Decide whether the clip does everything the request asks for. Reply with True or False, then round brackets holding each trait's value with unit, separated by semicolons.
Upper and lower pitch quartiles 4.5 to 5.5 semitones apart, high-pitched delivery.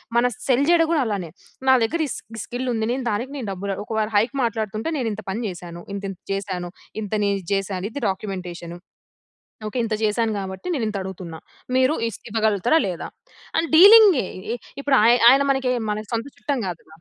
True (5.0 semitones; 215 Hz)